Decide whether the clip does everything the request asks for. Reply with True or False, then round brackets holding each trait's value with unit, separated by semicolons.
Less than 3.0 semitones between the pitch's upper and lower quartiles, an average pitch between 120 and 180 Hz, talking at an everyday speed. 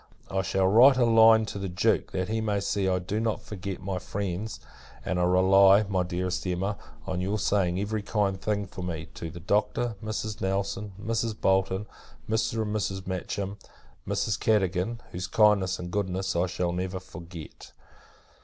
False (2.4 semitones; 95 Hz; 170 wpm)